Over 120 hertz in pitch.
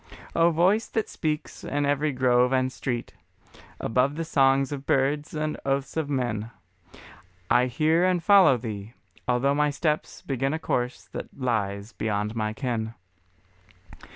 Yes: low, 135 Hz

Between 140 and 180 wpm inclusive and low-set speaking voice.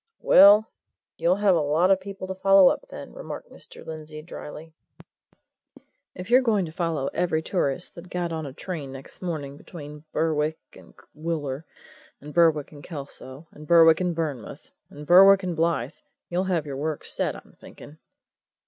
No: average, 165 wpm; medium, 165 Hz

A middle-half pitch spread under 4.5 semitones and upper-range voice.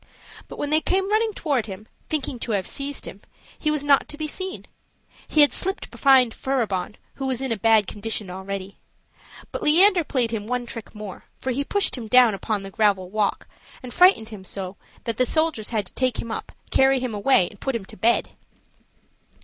No: wide, 5.4 semitones; high, 240 Hz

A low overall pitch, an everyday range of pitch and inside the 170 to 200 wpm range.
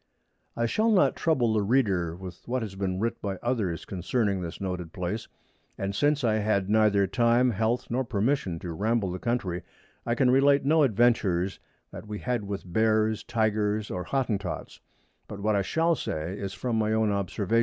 Yes: low, 110 Hz; average, 3.7 semitones; average, 180 wpm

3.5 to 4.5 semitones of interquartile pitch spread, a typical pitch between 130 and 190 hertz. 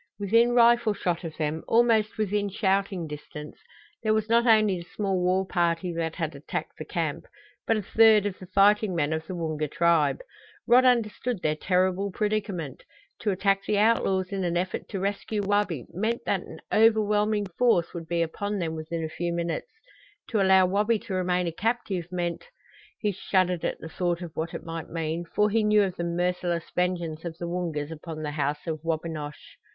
Yes: average, 3.9 semitones; medium, 185 Hz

